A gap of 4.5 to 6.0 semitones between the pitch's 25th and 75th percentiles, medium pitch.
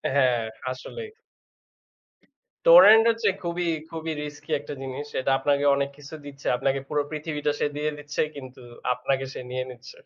No: average, 2.9 semitones; medium, 145 Hz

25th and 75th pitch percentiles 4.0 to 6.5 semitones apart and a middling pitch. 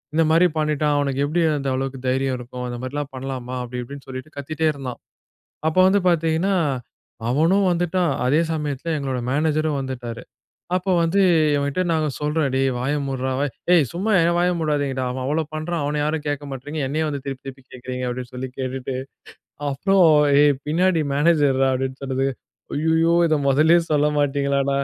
No: average, 3.1 semitones; medium, 145 Hz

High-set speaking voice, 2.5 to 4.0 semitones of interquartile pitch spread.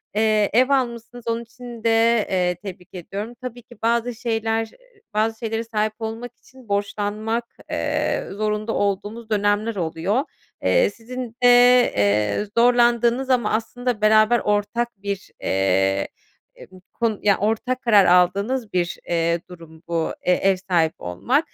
Yes: high, 220 Hz; average, 3.6 semitones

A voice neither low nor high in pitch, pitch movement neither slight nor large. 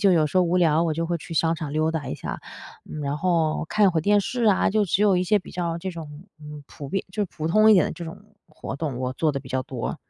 Yes: medium, 165 Hz; average, 3.7 semitones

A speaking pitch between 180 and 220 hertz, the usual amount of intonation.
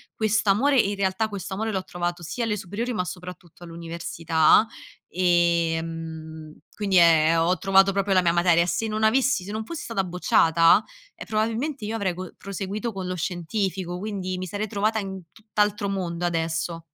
Yes: medium, 185 Hz; average, 3.6 semitones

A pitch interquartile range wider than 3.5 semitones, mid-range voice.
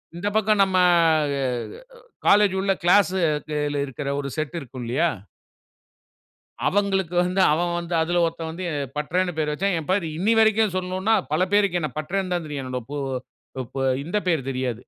Yes: average, 4.3 semitones; medium, 175 Hz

